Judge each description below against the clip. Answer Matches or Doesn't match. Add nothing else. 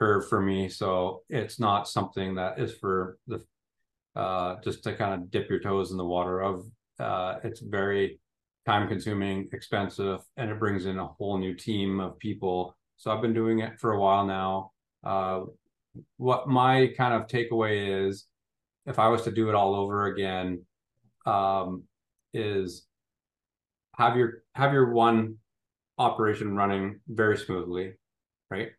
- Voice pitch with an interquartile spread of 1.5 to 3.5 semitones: Matches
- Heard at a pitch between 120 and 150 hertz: Doesn't match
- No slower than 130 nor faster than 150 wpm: Doesn't match